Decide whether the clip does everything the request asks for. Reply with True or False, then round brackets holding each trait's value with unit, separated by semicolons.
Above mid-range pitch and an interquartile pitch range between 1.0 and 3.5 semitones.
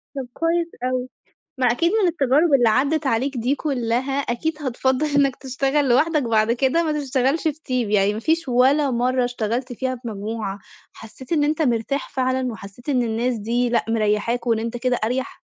True (255 Hz; 3.2 semitones)